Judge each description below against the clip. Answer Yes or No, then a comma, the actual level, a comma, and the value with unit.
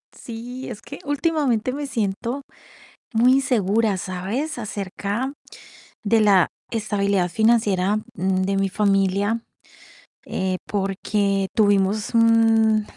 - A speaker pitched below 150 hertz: No, high, 215 Hz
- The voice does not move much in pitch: No, average, 3.0 semitones